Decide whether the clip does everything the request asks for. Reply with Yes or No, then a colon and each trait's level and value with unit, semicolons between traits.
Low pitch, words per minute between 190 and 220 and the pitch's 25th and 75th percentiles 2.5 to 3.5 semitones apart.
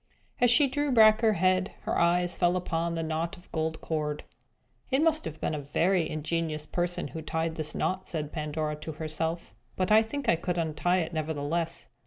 No: medium, 165 Hz; average, 195 wpm; average, 2.8 semitones